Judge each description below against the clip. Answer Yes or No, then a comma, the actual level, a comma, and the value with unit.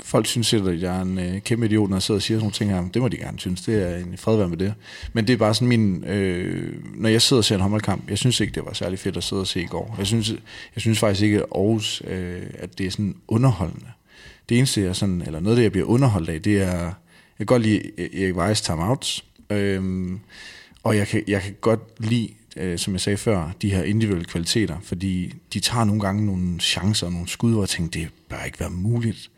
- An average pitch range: Yes, average, 3.2 semitones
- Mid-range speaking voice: No, low, 100 Hz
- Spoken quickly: Yes, fast, 260 wpm